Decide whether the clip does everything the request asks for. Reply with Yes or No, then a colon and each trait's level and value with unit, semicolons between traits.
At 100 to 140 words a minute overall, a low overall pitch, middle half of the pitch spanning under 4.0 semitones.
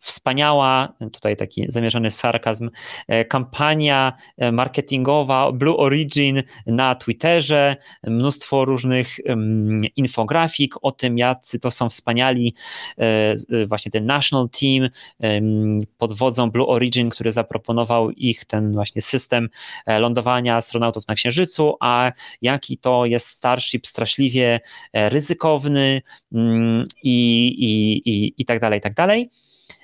Yes: slow, 110 wpm; low, 120 Hz; average, 2.9 semitones